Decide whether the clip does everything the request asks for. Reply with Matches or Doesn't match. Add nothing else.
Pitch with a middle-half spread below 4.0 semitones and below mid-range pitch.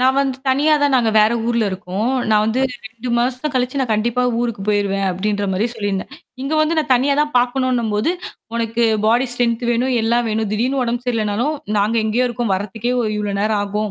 Doesn't match